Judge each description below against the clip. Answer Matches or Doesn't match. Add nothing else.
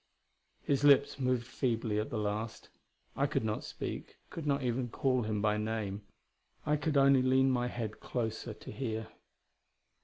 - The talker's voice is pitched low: Matches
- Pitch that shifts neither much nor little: Matches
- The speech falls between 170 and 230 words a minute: Doesn't match